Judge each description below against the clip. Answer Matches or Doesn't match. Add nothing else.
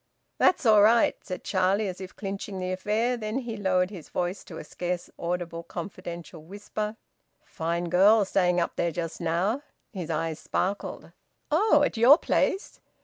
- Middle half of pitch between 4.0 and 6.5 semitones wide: Doesn't match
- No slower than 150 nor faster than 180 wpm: Matches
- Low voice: Doesn't match